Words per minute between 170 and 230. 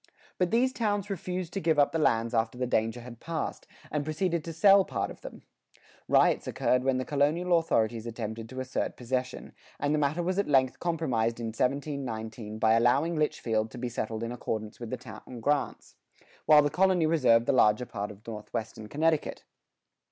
Yes: average, 185 wpm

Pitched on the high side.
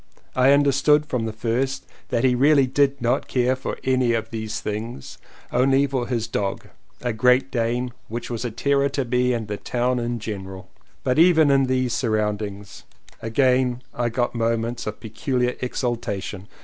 No: low, 125 Hz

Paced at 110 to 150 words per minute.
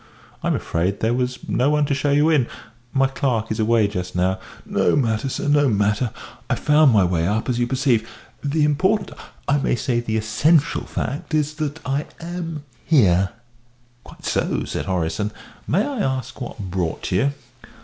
No: average, 180 wpm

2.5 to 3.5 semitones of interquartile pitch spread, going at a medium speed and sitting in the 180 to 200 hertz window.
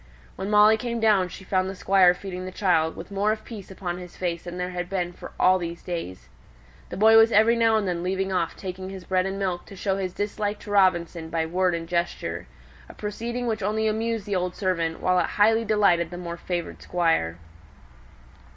No: average, 2.8 semitones; fast, 215 wpm; medium, 185 Hz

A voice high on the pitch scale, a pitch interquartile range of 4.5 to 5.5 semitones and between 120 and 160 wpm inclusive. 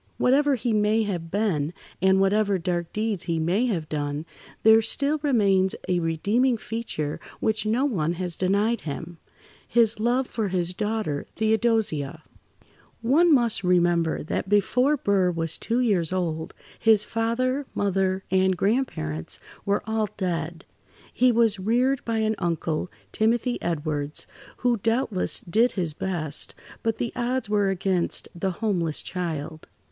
Yes: high, 200 Hz; average, 4.9 semitones; average, 140 wpm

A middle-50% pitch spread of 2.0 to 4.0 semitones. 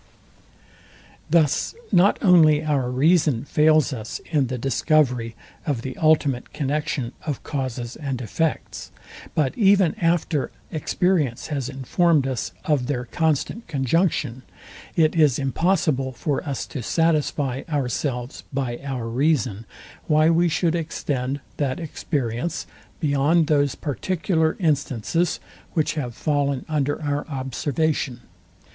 Yes: average, 3.5 semitones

